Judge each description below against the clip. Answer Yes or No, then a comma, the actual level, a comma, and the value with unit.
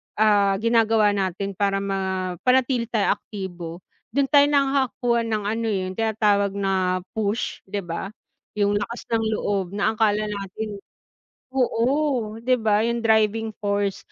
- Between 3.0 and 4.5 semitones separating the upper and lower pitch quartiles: No, narrow, 2.5 semitones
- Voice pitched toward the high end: Yes, high, 210 Hz